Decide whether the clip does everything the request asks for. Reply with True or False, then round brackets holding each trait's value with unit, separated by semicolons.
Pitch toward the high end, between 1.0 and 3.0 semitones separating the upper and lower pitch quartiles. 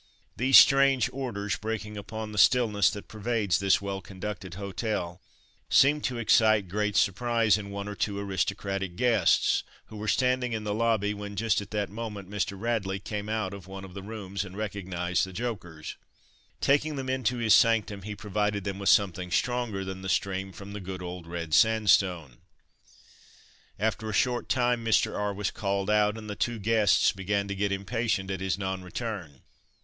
False (105 Hz; 2.5 semitones)